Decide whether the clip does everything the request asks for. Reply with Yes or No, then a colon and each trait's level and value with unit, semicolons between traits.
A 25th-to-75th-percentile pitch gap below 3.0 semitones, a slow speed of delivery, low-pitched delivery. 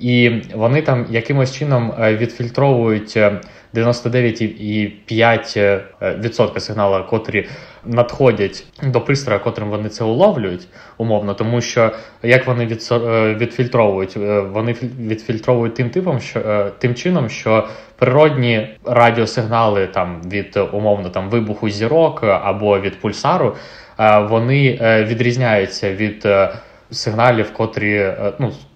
Yes: narrow, 2.6 semitones; slow, 100 wpm; low, 115 Hz